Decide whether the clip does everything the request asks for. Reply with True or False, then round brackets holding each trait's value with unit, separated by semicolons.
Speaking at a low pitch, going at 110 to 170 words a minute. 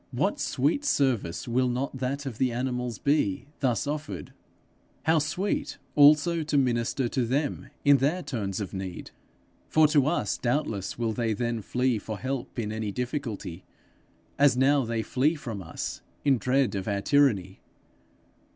True (125 Hz; 155 wpm)